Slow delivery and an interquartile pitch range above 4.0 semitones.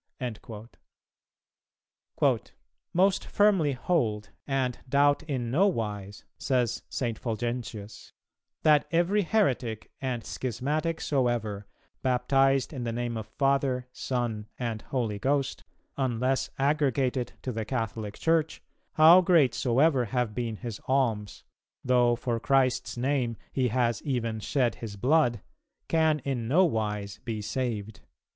No: slow, 120 wpm; average, 3.6 semitones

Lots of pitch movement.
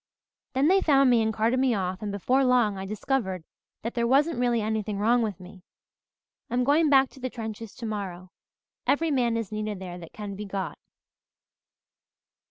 No: average, 4.2 semitones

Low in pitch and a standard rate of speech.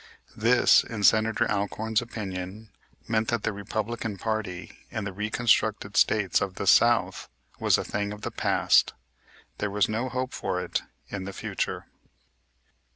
Yes: low, 105 Hz; average, 150 wpm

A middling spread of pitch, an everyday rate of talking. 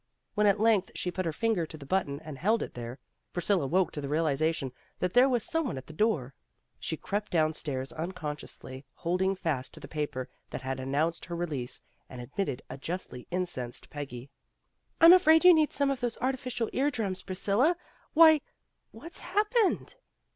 No: wide, 8.2 semitones; average, 185 wpm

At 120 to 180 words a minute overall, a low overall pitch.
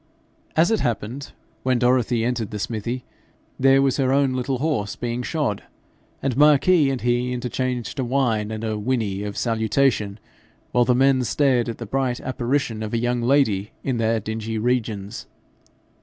Yes: average, 165 wpm; low, 120 Hz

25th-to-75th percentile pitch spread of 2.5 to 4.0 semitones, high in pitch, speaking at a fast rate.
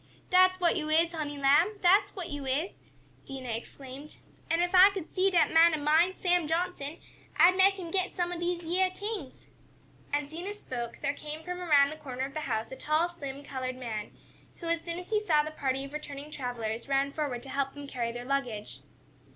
No: average, 4.4 semitones; very high, 305 Hz; fast, 210 wpm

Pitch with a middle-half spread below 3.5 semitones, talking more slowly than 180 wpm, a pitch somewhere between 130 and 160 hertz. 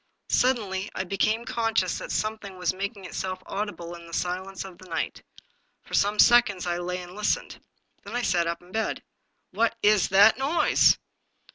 No: average, 3.1 semitones; average, 170 wpm; high, 195 Hz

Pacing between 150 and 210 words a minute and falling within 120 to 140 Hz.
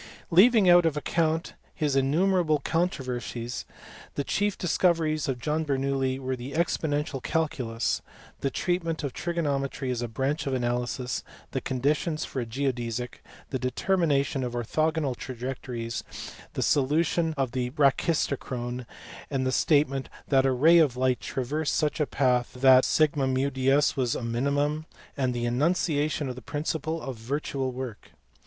No: average, 140 wpm; low, 135 Hz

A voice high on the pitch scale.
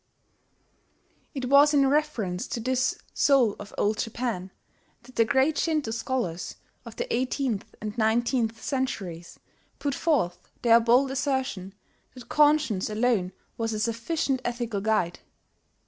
Yes: high, 235 Hz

